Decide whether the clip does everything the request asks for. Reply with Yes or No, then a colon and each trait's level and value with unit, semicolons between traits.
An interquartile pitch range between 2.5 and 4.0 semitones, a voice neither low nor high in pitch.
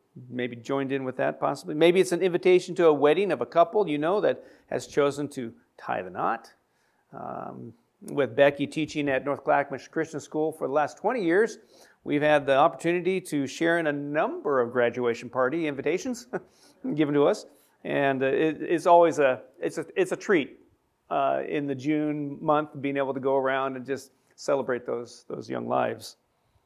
Yes: average, 3.0 semitones; medium, 145 Hz